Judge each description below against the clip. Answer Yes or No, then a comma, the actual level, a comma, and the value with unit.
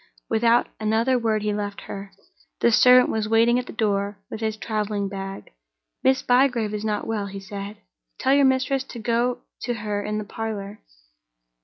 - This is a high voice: Yes, high, 220 Hz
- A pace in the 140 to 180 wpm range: Yes, average, 175 wpm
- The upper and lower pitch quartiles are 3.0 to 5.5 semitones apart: No, narrow, 2.6 semitones